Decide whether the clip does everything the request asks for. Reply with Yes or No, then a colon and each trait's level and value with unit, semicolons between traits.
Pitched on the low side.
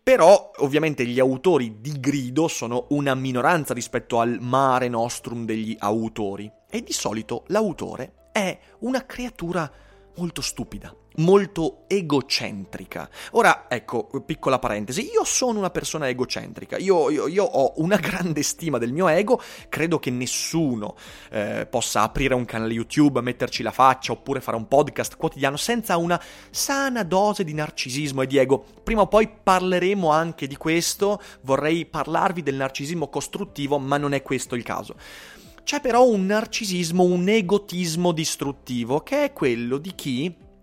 No: medium, 145 Hz